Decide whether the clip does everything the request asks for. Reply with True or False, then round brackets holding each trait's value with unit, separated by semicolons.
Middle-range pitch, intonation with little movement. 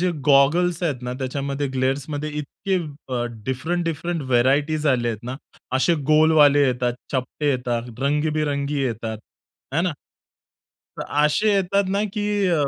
False (145 Hz; 3.9 semitones)